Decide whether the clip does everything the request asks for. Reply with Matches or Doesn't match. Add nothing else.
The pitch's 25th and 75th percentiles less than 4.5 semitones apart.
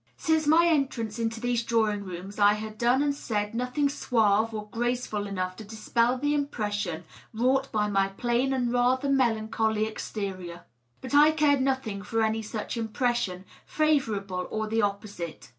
Matches